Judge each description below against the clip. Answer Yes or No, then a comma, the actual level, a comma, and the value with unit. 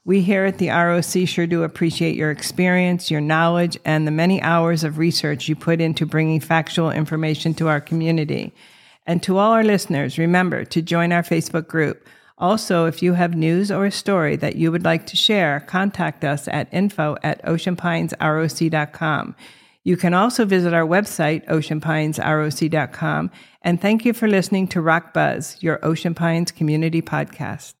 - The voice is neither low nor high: Yes, medium, 165 Hz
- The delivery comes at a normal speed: Yes, average, 170 wpm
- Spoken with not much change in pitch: Yes, narrow, 2.3 semitones